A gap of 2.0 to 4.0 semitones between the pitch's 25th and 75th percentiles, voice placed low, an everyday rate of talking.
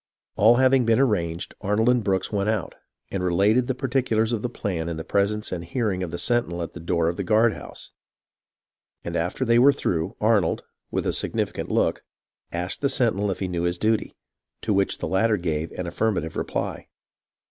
No: average, 4.8 semitones; low, 100 Hz; average, 195 wpm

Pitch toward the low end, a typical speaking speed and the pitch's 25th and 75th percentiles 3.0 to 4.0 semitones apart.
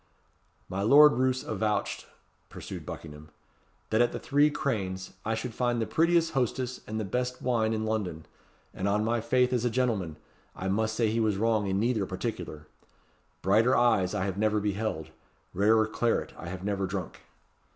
Yes: low, 110 Hz; average, 170 wpm; average, 3.7 semitones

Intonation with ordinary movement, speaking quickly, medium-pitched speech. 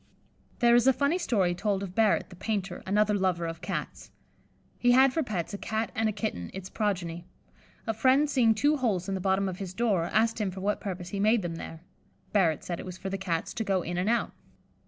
No: average, 3.8 semitones; fast, 230 wpm; high, 200 Hz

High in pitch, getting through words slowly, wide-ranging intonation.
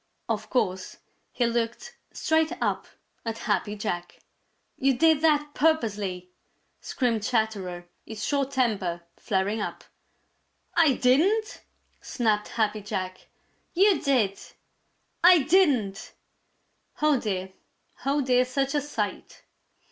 Yes: high, 235 Hz; slow, 110 wpm; wide, 5.9 semitones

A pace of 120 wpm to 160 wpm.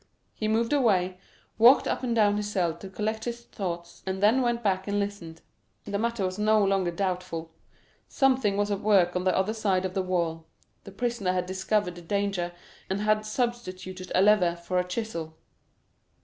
No: average, 185 wpm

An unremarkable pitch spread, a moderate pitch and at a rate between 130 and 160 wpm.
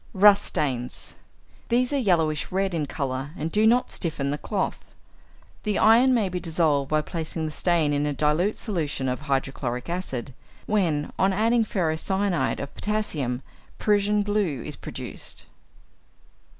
No: wide, 6.0 semitones; medium, 170 Hz; average, 145 wpm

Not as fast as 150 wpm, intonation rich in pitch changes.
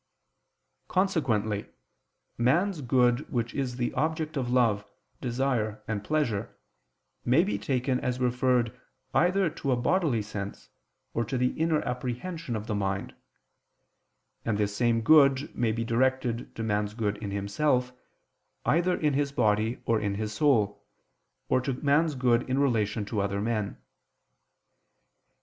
No: average, 140 wpm; average, 4.4 semitones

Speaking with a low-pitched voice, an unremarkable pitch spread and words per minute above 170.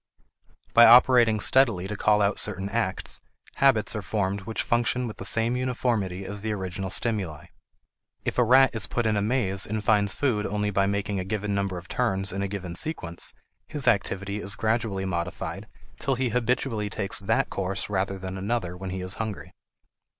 Yes: low, 105 Hz; average, 3.3 semitones; average, 185 wpm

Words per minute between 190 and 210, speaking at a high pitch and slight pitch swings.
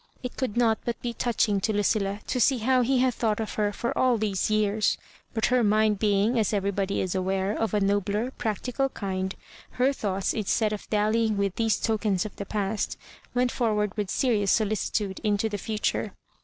Yes: average, 195 wpm; high, 215 Hz; narrow, 2.3 semitones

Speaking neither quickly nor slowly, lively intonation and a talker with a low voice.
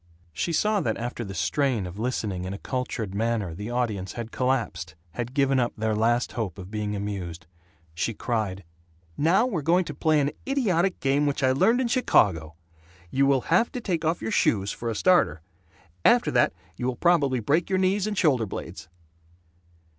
Yes: average, 185 wpm; wide, 7.7 semitones; low, 125 Hz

